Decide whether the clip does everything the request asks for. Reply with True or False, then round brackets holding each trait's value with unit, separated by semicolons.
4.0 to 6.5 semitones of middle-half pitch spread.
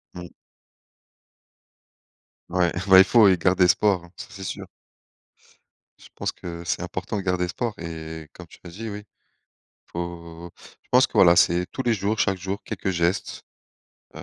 False (2.4 semitones)